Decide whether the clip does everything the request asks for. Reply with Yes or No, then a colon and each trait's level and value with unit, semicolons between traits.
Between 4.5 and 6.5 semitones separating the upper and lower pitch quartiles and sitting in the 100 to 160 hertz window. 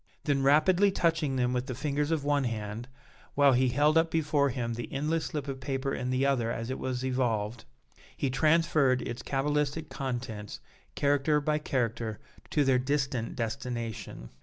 No: average, 3.3 semitones; low, 135 Hz